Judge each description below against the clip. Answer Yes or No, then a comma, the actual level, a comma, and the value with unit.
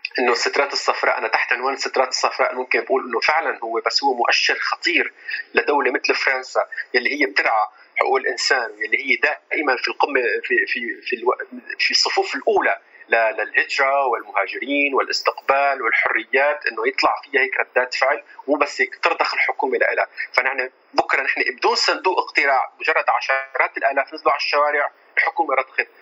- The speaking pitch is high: Yes, very high, 390 Hz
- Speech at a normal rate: No, fast, 155 wpm